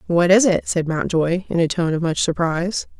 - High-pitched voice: No, medium, 170 Hz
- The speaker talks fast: Yes, fast, 220 wpm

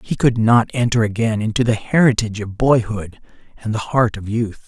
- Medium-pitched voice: No, low, 115 Hz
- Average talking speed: Yes, average, 190 wpm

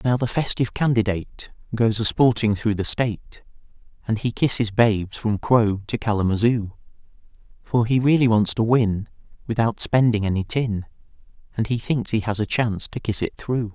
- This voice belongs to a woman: No, male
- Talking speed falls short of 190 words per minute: Yes, average, 170 wpm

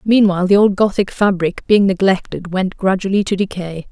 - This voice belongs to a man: No, female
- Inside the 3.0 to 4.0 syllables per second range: No, 5.3 syllables/s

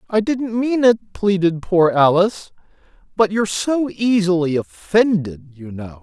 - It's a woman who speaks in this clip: No, male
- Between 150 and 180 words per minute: No, average, 140 wpm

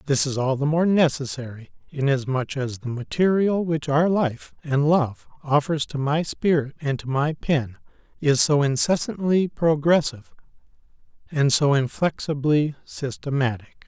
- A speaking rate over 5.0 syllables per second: No, 4.4 syllables/s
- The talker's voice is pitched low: No, medium, 145 Hz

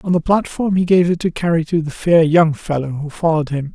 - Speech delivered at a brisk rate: Yes, fast, 255 wpm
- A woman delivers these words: No, male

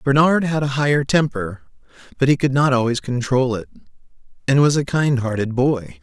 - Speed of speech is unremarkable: Yes, average, 180 wpm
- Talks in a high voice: No, low, 130 Hz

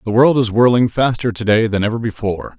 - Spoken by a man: Yes, male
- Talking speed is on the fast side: Yes, fast, 230 wpm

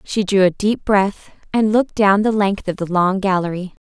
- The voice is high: Yes, high, 195 Hz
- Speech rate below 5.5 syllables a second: Yes, 4.9 syllables/s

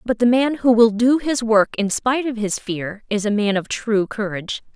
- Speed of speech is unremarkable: No, fast, 240 wpm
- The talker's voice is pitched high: Yes, high, 225 Hz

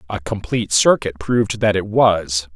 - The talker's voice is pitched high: No, low, 100 Hz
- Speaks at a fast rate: No, average, 165 wpm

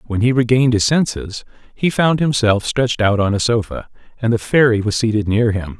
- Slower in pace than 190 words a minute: No, fast, 205 wpm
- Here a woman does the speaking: No, male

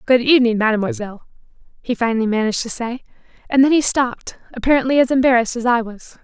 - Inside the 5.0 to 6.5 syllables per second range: No, 7.2 syllables/s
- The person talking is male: No, female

